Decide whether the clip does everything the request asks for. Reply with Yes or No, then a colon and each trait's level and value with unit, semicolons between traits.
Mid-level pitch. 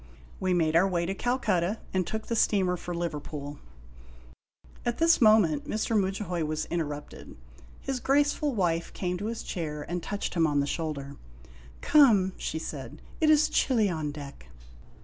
Yes: medium, 180 Hz